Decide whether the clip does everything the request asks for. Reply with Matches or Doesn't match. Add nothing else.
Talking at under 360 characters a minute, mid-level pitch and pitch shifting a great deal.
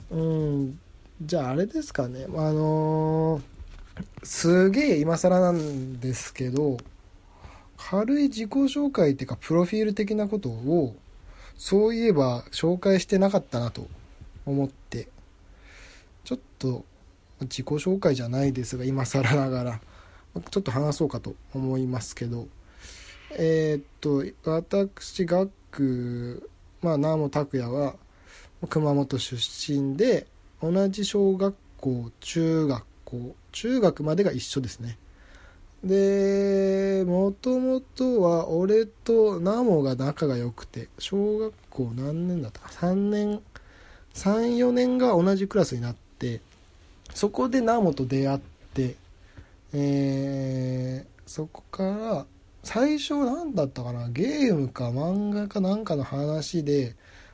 Matches